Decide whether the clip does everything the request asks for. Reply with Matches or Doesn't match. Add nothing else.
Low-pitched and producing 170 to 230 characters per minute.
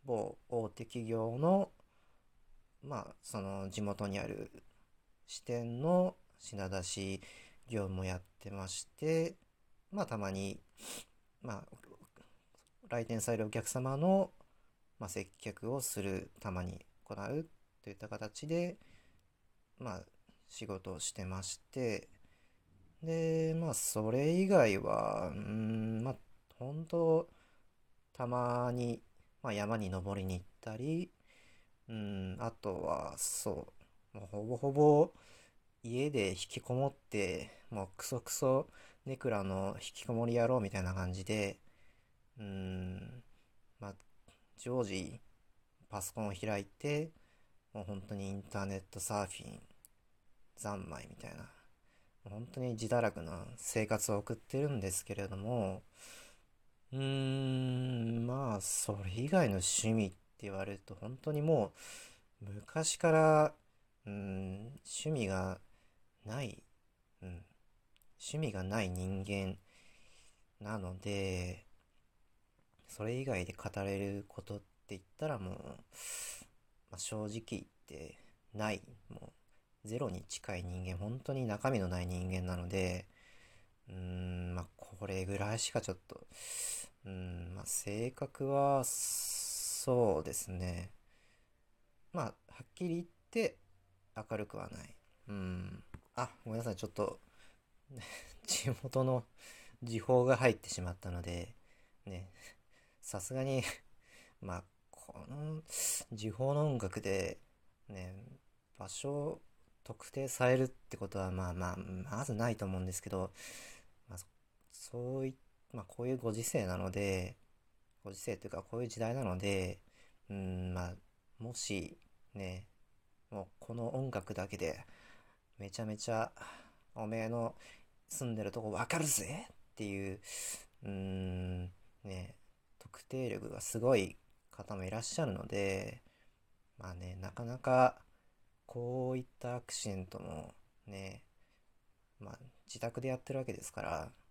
Matches